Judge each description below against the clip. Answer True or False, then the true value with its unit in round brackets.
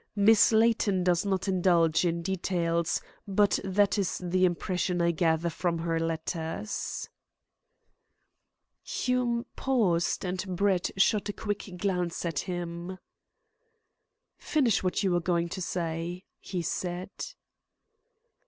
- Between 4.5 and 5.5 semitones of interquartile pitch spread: False (2.6 semitones)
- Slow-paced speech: True (115 wpm)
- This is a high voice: False (180 Hz)